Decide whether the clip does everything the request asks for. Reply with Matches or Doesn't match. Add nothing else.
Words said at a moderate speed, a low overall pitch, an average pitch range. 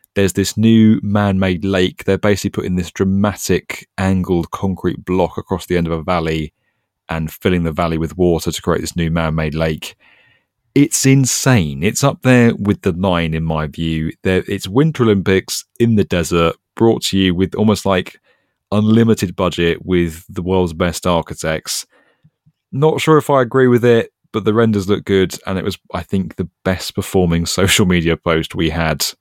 Matches